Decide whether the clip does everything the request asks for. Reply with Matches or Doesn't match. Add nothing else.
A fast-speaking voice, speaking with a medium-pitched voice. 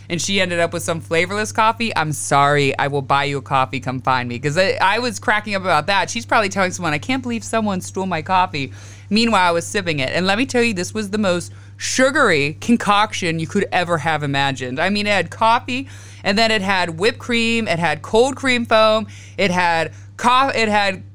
Matches